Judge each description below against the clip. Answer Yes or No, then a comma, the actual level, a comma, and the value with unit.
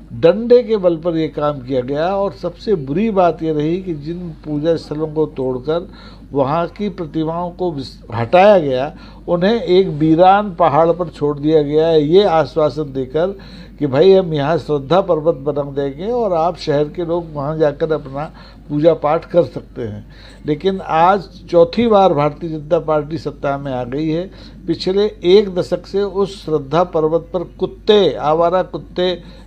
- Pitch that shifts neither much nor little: Yes, average, 3.3 semitones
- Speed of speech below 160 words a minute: No, average, 165 wpm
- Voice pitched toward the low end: No, medium, 165 Hz